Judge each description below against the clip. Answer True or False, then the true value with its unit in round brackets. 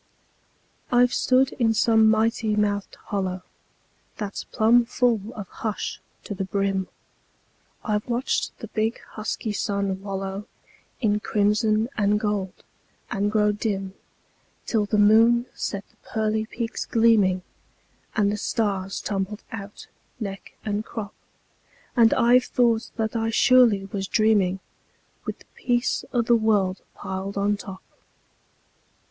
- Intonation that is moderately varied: False (2.2 semitones)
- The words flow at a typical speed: False (130 wpm)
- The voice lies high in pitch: True (210 Hz)